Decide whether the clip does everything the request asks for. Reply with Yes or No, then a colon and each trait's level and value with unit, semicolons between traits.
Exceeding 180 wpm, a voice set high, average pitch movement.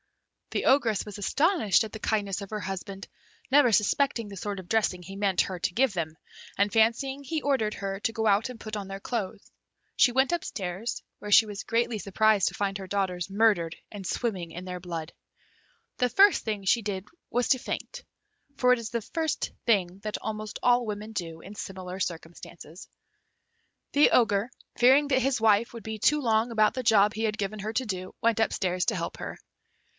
Yes: average, 200 wpm; high, 215 Hz; average, 3.3 semitones